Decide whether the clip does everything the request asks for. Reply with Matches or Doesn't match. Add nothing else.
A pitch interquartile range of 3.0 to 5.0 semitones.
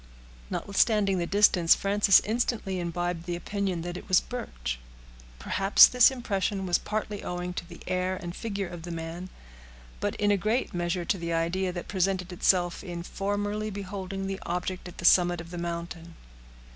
Doesn't match